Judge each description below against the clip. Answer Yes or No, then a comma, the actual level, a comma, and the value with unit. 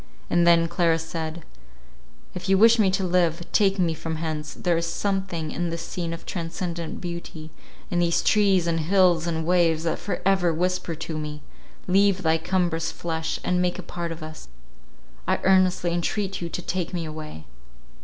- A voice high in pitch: No, medium, 170 Hz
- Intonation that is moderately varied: No, narrow, 2.0 semitones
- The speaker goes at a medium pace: Yes, average, 180 wpm